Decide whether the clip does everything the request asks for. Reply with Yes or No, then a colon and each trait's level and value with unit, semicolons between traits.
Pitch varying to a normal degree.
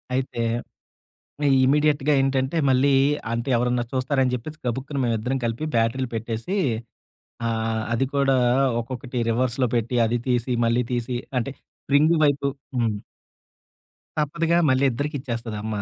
Yes: average, 3.0 semitones